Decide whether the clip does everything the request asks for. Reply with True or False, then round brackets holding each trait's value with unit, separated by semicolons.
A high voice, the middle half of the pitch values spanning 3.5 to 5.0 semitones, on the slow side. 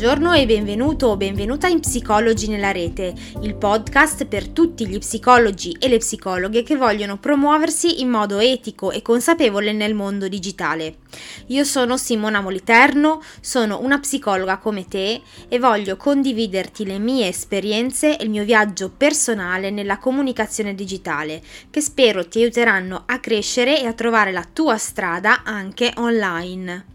False (220 Hz; 4.4 semitones; 145 wpm)